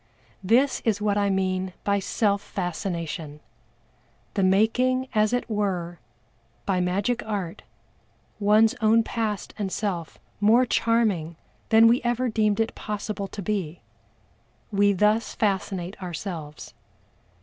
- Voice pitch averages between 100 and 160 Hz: No, high, 205 Hz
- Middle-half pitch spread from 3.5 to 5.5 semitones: No, average, 3.0 semitones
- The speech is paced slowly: Yes, slow, 120 wpm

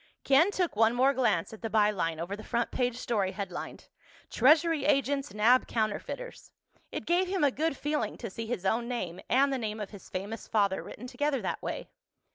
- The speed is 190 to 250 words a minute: Yes, average, 200 wpm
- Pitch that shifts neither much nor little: Yes, average, 4.9 semitones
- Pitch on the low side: No, high, 235 Hz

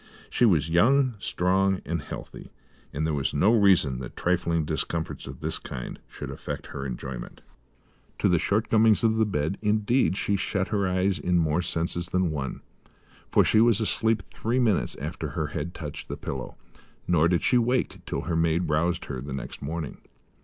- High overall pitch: No, very low, 85 Hz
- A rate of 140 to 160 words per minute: No, average, 180 wpm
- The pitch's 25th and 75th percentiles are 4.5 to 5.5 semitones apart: Yes, average, 5.1 semitones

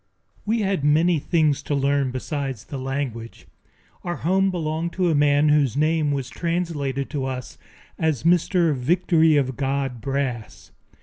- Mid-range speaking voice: Yes, medium, 145 Hz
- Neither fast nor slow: Yes, average, 145 wpm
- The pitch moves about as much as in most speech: Yes, average, 3.7 semitones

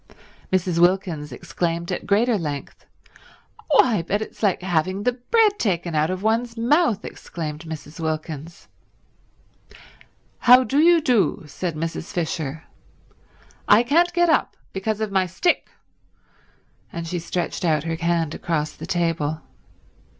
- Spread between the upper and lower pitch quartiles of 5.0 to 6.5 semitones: Yes, wide, 5.6 semitones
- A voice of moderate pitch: Yes, medium, 180 Hz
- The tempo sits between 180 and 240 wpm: No, slow, 135 wpm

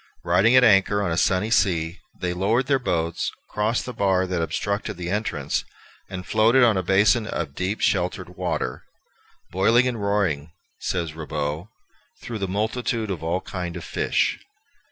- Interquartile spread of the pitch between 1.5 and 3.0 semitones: No, average, 4.0 semitones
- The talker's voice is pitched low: Yes, very low, 95 Hz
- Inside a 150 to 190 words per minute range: Yes, average, 165 wpm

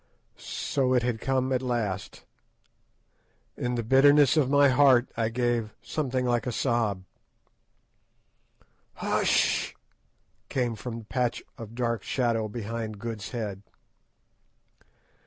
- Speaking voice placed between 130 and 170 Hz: No, low, 120 Hz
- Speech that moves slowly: Yes, slow, 115 wpm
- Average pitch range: No, narrow, 2.3 semitones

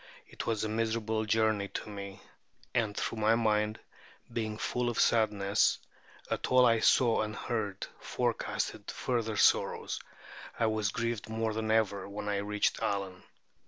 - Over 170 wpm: No, average, 150 wpm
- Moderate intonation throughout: No, narrow, 1.6 semitones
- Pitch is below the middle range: Yes, low, 110 Hz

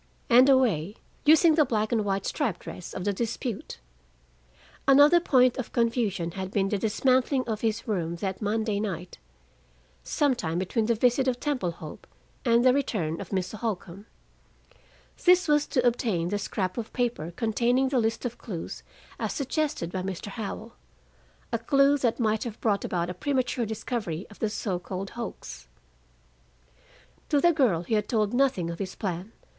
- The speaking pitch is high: Yes, high, 220 Hz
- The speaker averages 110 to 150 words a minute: No, average, 170 wpm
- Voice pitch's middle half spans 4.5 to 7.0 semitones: Yes, average, 4.9 semitones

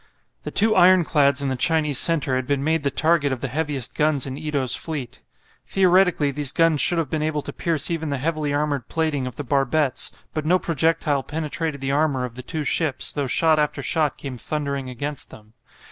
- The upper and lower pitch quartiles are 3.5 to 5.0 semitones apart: No, average, 2.7 semitones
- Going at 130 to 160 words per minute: No, fast, 205 wpm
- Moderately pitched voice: Yes, medium, 150 Hz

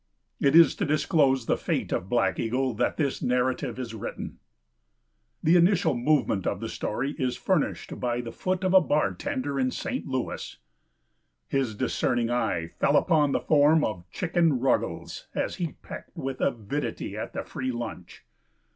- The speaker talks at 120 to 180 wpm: Yes, average, 160 wpm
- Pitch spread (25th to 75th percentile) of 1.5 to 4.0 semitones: No, average, 4.4 semitones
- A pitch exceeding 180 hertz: No, low, 135 Hz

